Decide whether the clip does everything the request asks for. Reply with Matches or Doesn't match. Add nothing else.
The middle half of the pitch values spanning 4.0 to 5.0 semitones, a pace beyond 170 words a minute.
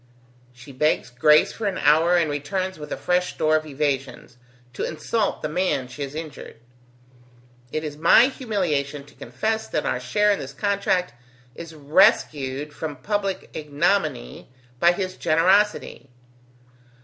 Doesn't match